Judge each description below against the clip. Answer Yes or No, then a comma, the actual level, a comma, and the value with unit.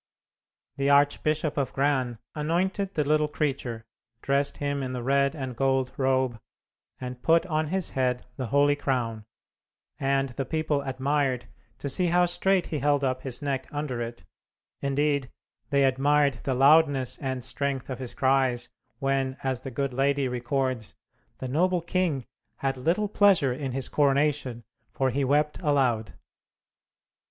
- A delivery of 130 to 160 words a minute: Yes, average, 150 wpm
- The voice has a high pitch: No, low, 135 Hz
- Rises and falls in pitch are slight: Yes, narrow, 2.3 semitones